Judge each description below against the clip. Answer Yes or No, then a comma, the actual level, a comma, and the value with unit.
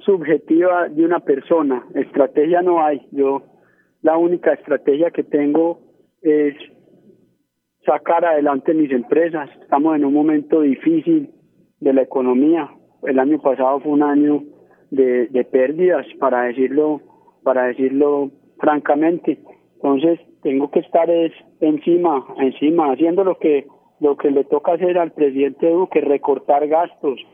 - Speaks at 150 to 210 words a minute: No, average, 130 wpm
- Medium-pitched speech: Yes, medium, 150 Hz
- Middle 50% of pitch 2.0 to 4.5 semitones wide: Yes, average, 3.3 semitones